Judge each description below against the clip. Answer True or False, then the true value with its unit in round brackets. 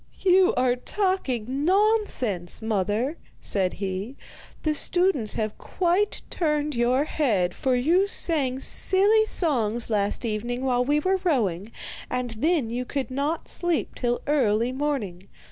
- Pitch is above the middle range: True (260 Hz)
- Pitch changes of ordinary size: False (6.9 semitones)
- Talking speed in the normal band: False (130 wpm)